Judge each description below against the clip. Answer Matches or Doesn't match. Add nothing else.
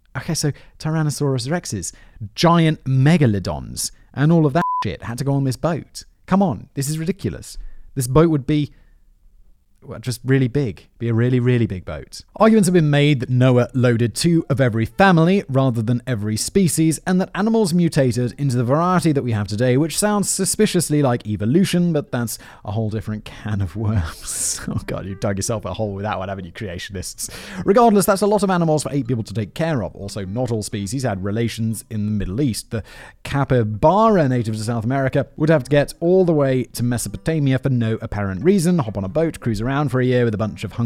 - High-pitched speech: Doesn't match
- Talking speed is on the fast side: Matches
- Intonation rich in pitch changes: Matches